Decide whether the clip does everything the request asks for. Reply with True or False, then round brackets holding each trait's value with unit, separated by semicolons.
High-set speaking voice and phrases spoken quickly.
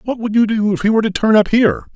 True (205 Hz; 340 wpm)